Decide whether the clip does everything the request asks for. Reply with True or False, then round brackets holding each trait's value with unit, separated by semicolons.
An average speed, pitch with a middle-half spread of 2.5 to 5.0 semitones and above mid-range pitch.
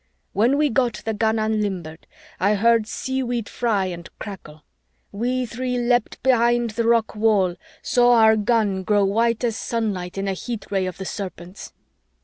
True (160 wpm; 3.3 semitones; 220 Hz)